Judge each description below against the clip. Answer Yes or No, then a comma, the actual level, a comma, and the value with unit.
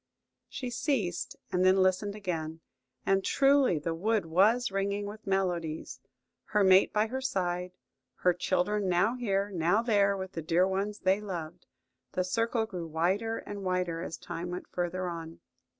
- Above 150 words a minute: Yes, average, 160 wpm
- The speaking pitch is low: No, high, 190 Hz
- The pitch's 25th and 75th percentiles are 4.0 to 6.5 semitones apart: No, average, 3.0 semitones